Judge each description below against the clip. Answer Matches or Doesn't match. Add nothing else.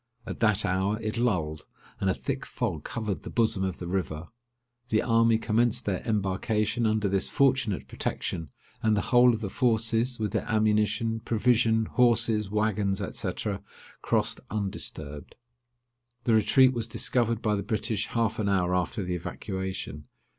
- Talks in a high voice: Doesn't match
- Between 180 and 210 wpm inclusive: Doesn't match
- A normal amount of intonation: Matches